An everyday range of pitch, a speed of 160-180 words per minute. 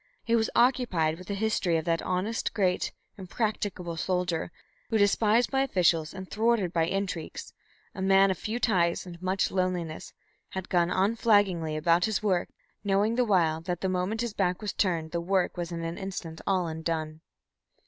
Yes: average, 3.3 semitones; average, 175 wpm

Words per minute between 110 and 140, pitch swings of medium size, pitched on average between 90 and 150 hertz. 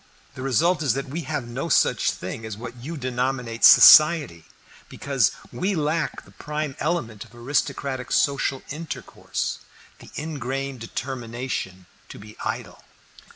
Yes: slow, 135 wpm; average, 4.3 semitones; low, 135 Hz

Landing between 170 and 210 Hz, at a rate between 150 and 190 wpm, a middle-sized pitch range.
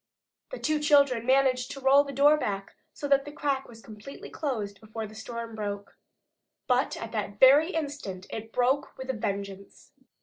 No: very high, 250 Hz; average, 175 wpm; average, 4.6 semitones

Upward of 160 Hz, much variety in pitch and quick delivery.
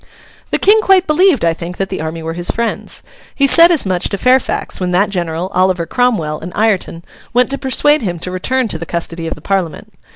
Yes: high, 190 Hz; wide, 7.4 semitones; fast, 220 wpm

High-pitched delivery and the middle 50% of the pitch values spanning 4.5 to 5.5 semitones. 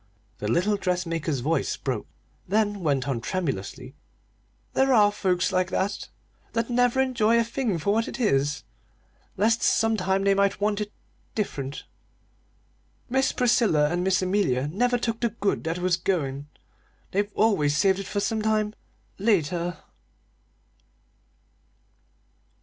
Yes: high, 195 Hz; average, 4.9 semitones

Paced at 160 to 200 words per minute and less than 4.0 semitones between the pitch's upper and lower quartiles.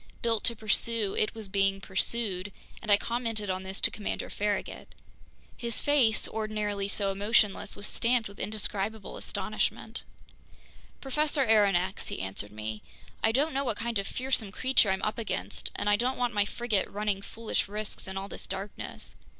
Yes: average, 165 wpm; average, 2.8 semitones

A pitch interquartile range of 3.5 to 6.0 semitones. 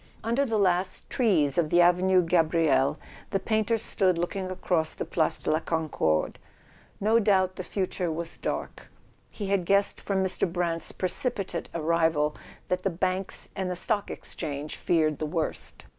No: average, 3.0 semitones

